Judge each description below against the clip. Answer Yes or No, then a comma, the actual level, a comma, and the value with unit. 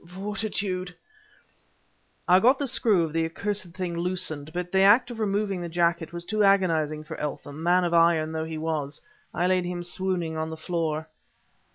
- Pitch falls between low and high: Yes, medium, 175 Hz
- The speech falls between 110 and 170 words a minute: No, average, 180 wpm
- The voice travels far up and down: No, average, 3.1 semitones